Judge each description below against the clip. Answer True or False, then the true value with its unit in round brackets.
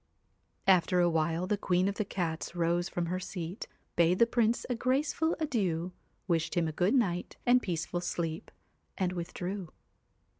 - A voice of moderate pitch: True (180 Hz)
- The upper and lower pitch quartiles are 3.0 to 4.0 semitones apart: True (3.4 semitones)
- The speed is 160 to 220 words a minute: True (165 wpm)